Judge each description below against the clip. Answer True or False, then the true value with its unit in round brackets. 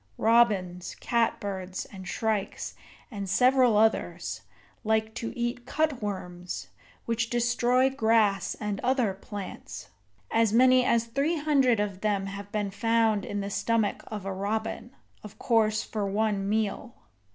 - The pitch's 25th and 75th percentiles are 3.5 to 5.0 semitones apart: False (3.0 semitones)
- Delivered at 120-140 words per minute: True (135 wpm)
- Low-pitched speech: False (220 Hz)